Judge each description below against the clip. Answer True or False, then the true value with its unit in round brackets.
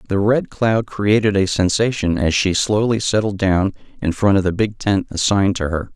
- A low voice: True (100 Hz)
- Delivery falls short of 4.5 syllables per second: False (5.0 syllables/s)